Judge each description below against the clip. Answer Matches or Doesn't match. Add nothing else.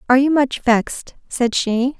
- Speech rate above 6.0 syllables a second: Doesn't match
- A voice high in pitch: Matches